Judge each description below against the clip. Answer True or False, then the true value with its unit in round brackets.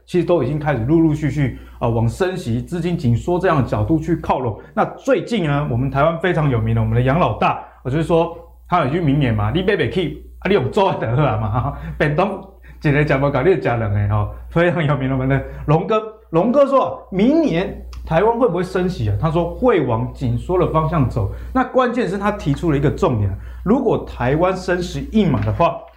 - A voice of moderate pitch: True (160 Hz)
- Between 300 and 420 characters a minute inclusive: True (320 characters per minute)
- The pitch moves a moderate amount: False (6.1 semitones)